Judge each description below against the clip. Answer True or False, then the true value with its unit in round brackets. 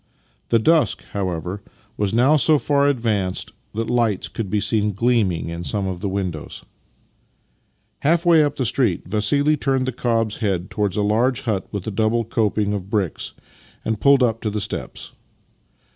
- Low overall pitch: True (110 Hz)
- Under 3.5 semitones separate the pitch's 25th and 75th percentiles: False (4.1 semitones)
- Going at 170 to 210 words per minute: True (175 wpm)